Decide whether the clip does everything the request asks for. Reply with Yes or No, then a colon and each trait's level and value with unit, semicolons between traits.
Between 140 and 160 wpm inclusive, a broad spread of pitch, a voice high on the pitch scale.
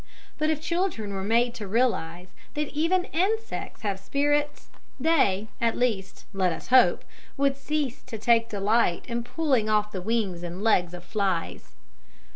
Yes: average, 155 wpm; wide, 6.7 semitones; high, 230 Hz